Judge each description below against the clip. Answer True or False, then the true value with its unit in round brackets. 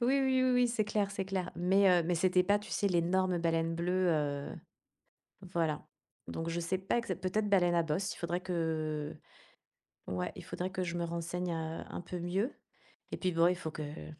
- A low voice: False (175 Hz)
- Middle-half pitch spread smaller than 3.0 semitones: True (2.6 semitones)